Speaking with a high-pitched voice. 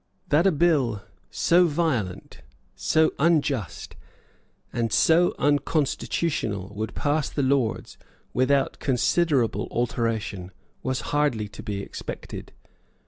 No: low, 135 Hz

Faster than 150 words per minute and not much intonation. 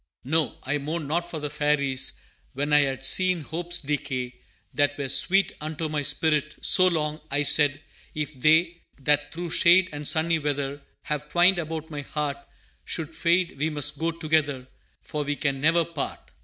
Yes: average, 170 wpm; narrow, 2.2 semitones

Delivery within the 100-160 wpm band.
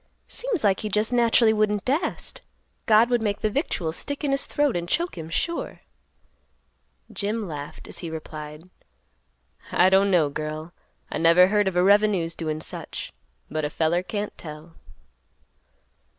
Yes: average, 155 wpm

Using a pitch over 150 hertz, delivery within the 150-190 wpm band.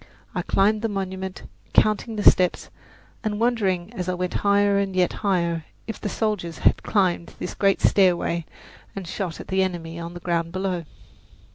Yes: high, 190 Hz; average, 170 wpm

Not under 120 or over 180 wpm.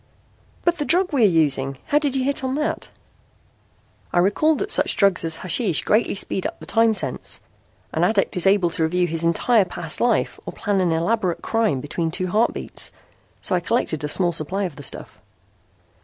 No: average, 195 wpm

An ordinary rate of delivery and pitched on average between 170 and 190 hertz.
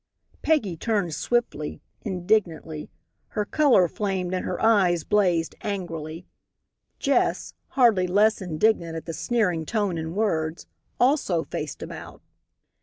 No: slow, 115 wpm; medium, 185 Hz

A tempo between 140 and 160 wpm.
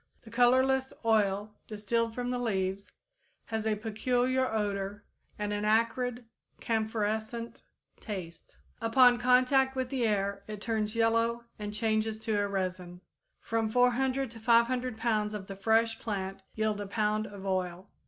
Yes: average, 145 wpm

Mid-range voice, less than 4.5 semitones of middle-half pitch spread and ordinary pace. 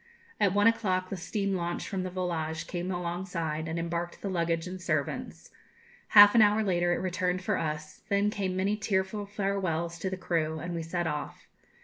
Yes: medium, 180 Hz; average, 2.7 semitones; average, 190 wpm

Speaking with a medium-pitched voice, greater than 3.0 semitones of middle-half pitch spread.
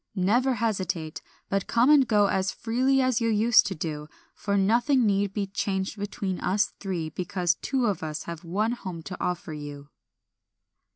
No: high, 195 Hz; average, 4.3 semitones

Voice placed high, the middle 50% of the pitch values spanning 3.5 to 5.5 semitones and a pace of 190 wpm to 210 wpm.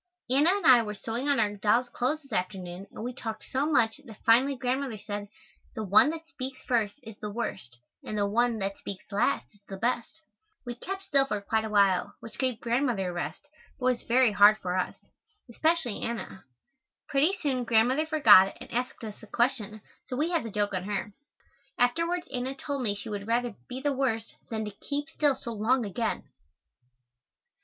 Yes: high, 235 Hz; average, 4.4 semitones; average, 195 wpm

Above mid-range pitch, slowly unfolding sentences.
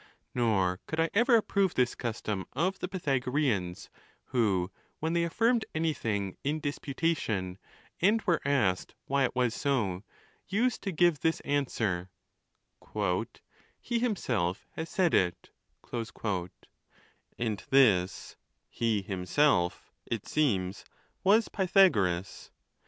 No: low, 135 Hz; slow, 120 wpm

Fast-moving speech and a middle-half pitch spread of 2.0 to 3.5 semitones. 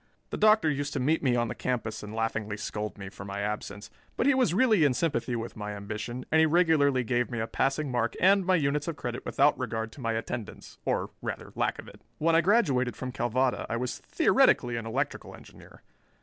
No: fast, 220 wpm; average, 5.3 semitones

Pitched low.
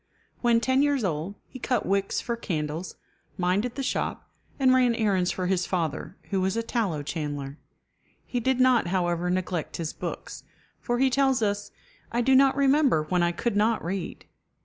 No: high, 200 Hz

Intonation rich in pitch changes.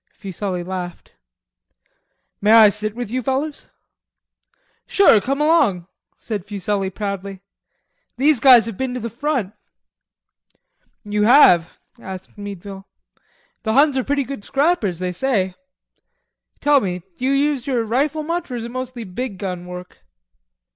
Yes: wide, 5.7 semitones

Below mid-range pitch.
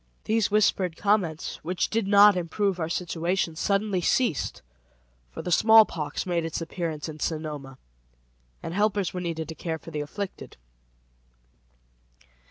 No: medium, 175 Hz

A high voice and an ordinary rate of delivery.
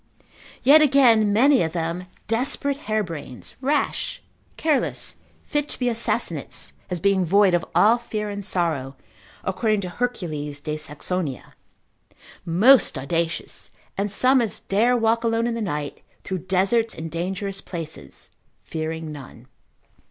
No: high, 195 Hz; slow, 130 wpm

